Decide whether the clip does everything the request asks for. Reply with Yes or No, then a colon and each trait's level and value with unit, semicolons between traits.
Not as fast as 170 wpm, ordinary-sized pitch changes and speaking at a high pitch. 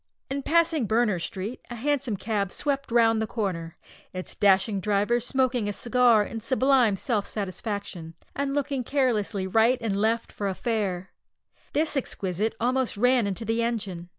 Yes: average, 155 wpm; average, 4.1 semitones; high, 225 Hz